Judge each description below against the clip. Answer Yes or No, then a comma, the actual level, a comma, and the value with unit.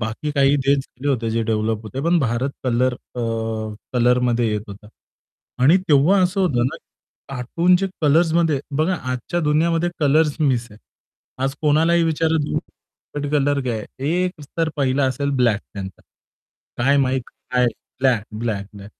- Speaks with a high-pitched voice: No, low, 135 Hz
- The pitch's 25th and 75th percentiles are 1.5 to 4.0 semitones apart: No, average, 5.0 semitones